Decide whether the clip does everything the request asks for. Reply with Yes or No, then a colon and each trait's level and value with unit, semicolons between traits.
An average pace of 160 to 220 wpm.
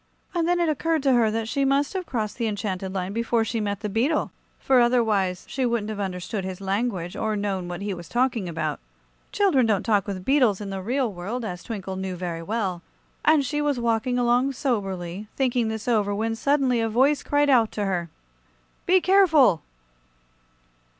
Yes: average, 190 wpm